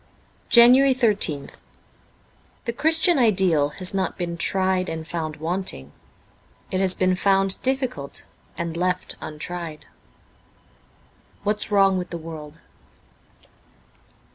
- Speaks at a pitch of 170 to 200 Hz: Yes, medium, 185 Hz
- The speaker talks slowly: Yes, slow, 115 wpm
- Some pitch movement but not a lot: Yes, average, 4.1 semitones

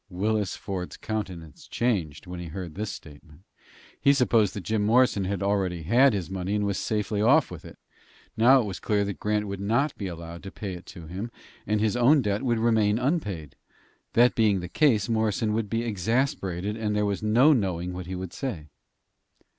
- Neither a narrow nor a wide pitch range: Yes, average, 3.6 semitones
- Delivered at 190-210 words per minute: Yes, average, 195 wpm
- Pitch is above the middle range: No, low, 105 Hz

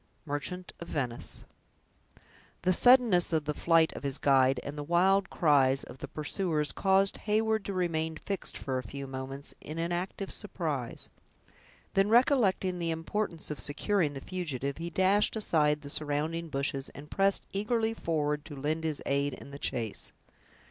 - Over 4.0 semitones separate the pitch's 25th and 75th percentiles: Yes, average, 4.9 semitones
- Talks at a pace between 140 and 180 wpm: Yes, average, 160 wpm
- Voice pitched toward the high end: No, medium, 160 Hz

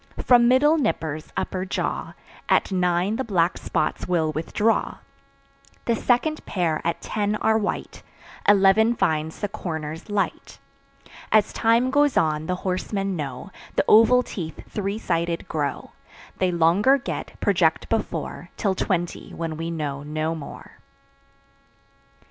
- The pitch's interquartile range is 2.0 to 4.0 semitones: No, average, 5.2 semitones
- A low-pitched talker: No, medium, 185 Hz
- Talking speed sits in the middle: No, slow, 130 wpm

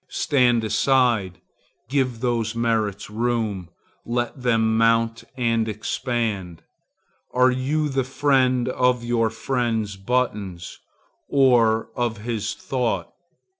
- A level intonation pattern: Yes, narrow, 2.2 semitones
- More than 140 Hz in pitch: No, low, 115 Hz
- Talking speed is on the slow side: Yes, slow, 100 wpm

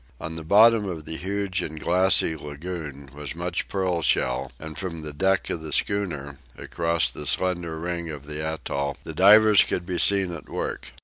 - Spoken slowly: No, average, 185 wpm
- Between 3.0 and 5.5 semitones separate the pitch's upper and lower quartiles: Yes, average, 3.5 semitones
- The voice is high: No, very low, 85 Hz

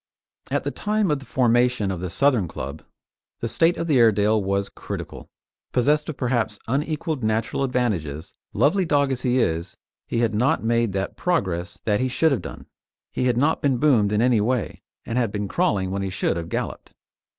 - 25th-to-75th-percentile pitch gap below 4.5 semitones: No, average, 5.3 semitones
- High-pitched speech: No, low, 120 Hz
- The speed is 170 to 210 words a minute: Yes, average, 195 wpm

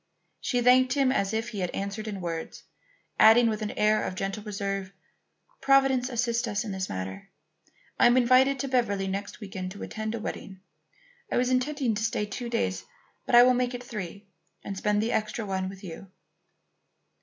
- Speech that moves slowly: No, average, 190 wpm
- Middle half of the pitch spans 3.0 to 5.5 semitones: Yes, average, 3.9 semitones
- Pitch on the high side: Yes, high, 215 Hz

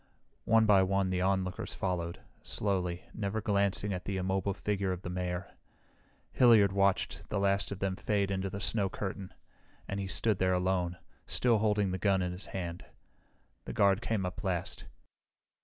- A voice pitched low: Yes, very low, 95 Hz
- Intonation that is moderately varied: No, narrow, 1.6 semitones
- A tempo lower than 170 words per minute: No, average, 175 wpm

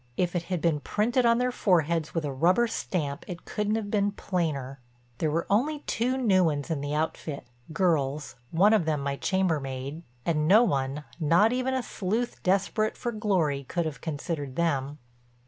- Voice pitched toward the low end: No, medium, 170 Hz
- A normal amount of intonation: No, wide, 6.1 semitones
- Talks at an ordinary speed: Yes, average, 170 wpm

